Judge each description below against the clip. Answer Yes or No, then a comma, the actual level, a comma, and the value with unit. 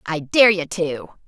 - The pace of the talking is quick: No, average, 190 wpm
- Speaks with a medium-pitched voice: Yes, medium, 170 Hz